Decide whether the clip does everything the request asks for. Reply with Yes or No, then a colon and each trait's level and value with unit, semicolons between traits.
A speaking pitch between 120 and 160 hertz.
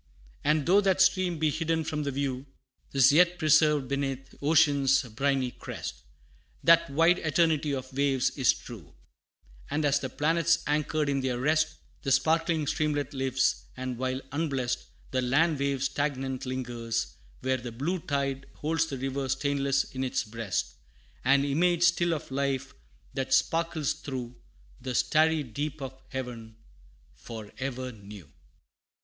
Yes: medium, 140 Hz